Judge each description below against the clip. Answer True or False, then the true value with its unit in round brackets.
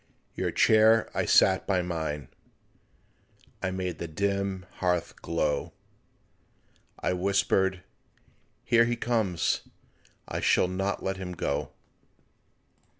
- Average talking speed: False (105 wpm)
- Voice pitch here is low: True (95 Hz)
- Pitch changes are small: True (2.0 semitones)